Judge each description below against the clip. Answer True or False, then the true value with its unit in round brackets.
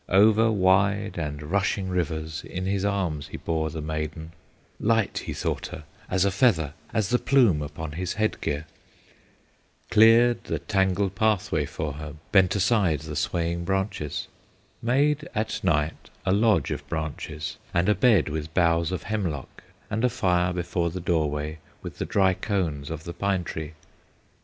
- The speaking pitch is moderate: False (90 Hz)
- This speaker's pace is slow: False (160 wpm)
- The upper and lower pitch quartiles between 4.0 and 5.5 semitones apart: True (4.5 semitones)